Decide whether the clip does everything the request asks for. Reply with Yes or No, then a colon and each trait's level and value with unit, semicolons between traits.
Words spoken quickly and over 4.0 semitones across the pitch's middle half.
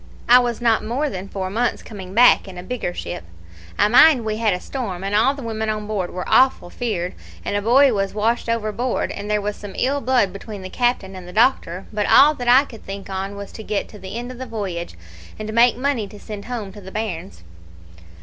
No: fast, 235 wpm; average, 3.7 semitones